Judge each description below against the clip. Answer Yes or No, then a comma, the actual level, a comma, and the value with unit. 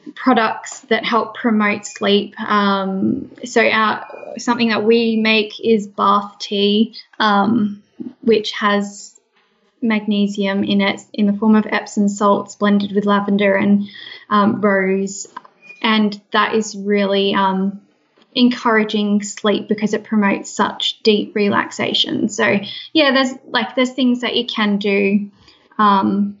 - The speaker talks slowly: Yes, slow, 130 wpm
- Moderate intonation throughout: No, narrow, 1.8 semitones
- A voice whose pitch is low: No, high, 210 Hz